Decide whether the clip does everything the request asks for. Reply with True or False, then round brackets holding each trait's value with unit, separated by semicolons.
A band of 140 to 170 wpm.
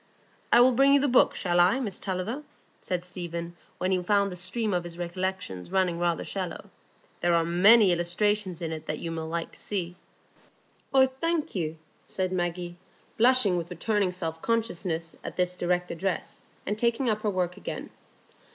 False (180 wpm)